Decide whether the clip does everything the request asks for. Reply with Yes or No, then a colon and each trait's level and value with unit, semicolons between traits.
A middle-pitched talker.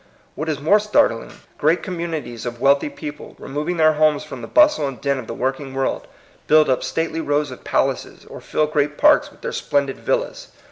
Yes: medium, 150 Hz